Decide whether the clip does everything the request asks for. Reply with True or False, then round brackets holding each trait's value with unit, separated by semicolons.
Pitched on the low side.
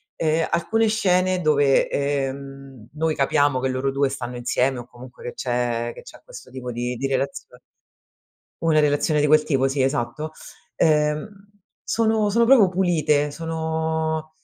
False (145 Hz)